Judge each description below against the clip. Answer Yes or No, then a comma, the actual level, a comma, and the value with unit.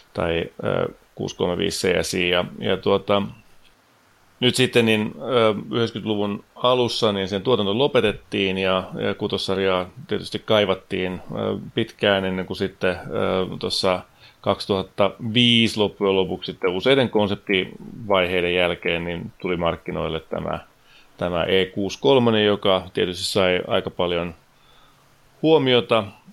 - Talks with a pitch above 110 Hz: No, very low, 95 Hz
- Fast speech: No, slow, 95 wpm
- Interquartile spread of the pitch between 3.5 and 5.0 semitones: No, average, 2.9 semitones